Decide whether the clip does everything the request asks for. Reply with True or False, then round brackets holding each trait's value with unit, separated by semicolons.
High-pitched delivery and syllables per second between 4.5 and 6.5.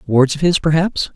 False (155 Hz; 5.0 syllables/s)